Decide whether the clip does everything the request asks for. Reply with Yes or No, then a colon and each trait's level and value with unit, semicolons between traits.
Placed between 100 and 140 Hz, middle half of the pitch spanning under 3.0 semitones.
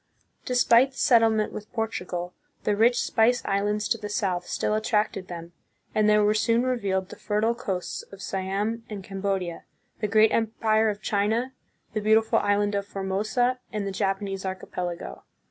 No: high, 210 Hz; narrow, 2.4 semitones